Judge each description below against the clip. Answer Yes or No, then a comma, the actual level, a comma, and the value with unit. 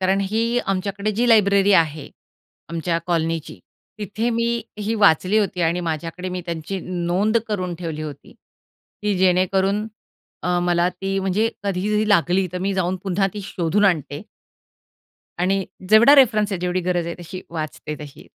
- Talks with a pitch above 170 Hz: Yes, medium, 185 Hz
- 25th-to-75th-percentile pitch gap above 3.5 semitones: No, average, 3.1 semitones